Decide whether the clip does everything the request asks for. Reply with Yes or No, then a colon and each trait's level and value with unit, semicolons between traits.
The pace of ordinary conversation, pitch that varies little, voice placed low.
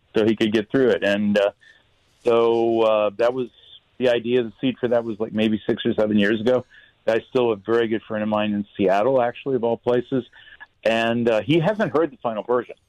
No: fast, 230 wpm; narrow, 2.3 semitones; low, 115 Hz